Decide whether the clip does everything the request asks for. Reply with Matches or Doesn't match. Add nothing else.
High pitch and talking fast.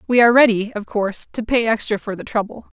Matches